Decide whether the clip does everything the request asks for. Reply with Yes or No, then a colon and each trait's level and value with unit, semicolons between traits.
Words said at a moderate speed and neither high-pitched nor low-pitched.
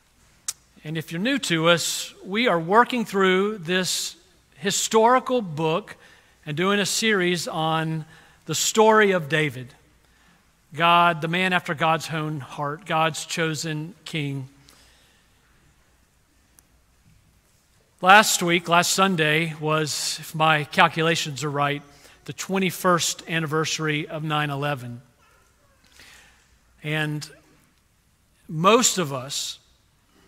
No: slow, 105 wpm; medium, 160 Hz